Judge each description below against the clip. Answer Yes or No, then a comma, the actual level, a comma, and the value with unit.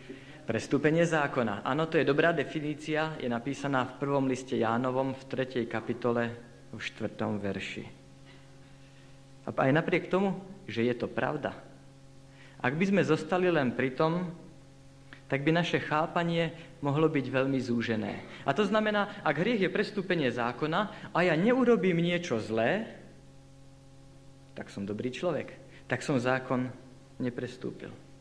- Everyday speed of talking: Yes, average, 135 wpm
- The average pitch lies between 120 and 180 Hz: Yes, low, 135 Hz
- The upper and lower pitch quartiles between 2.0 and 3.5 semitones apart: No, average, 4.0 semitones